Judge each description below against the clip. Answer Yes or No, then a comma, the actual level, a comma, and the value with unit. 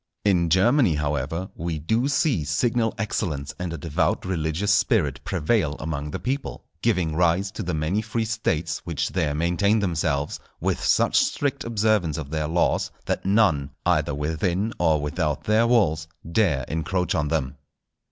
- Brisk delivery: No, average, 155 wpm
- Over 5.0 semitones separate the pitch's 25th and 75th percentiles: Yes, wide, 5.5 semitones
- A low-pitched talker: Yes, very low, 85 Hz